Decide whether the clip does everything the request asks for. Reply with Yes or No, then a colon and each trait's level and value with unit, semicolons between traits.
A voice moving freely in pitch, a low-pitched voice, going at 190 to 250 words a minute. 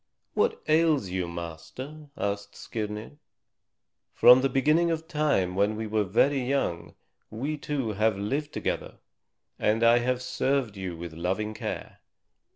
No: wide, 6.3 semitones; low, 115 Hz; average, 140 wpm